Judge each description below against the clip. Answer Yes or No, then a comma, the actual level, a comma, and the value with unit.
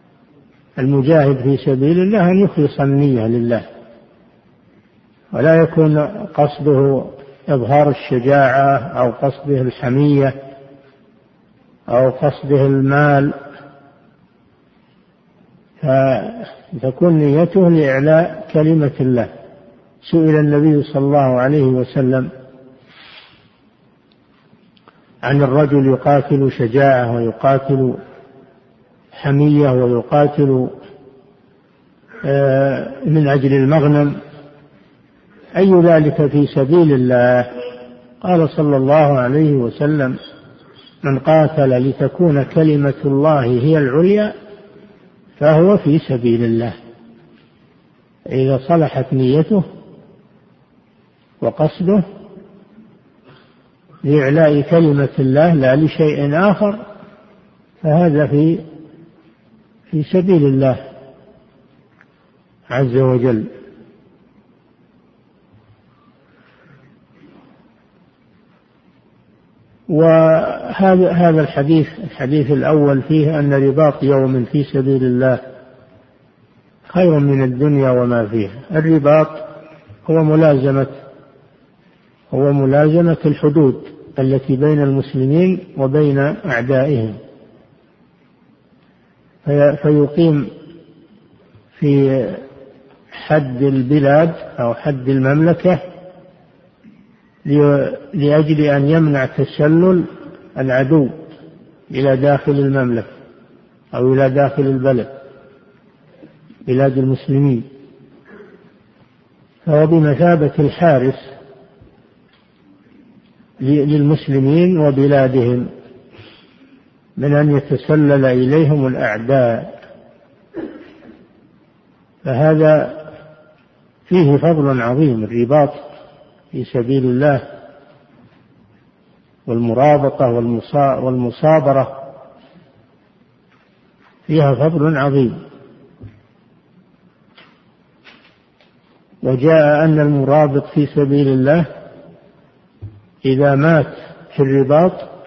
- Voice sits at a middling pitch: Yes, medium, 145 Hz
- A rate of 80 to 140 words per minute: No, slow, 65 wpm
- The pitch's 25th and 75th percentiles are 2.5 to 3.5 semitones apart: Yes, average, 2.8 semitones